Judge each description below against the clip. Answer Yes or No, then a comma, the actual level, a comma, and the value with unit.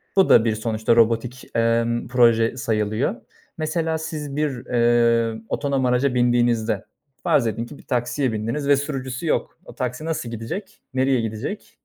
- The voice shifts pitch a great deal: No, average, 3.3 semitones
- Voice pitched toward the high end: No, low, 120 Hz